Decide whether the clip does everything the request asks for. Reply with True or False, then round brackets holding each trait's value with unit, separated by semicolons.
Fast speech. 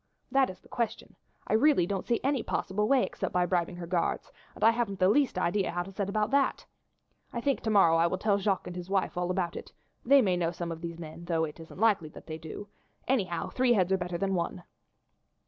True (240 wpm)